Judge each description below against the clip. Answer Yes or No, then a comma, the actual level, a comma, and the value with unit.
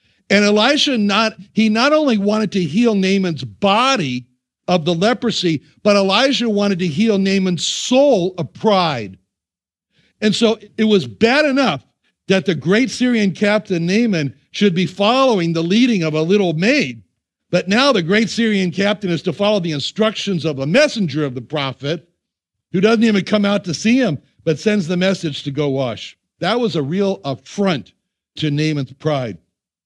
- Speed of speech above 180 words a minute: No, average, 170 wpm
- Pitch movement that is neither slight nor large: No, wide, 5.8 semitones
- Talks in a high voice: Yes, high, 195 Hz